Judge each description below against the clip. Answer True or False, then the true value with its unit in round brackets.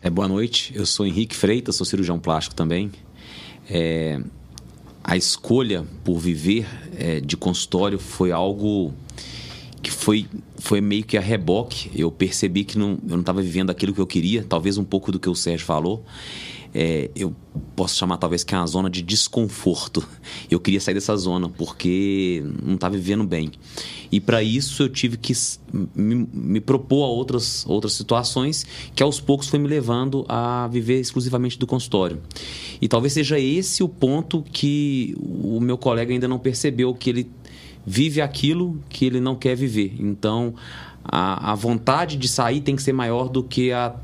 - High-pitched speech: False (105 Hz)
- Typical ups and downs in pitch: False (5.9 semitones)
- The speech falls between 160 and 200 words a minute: True (175 wpm)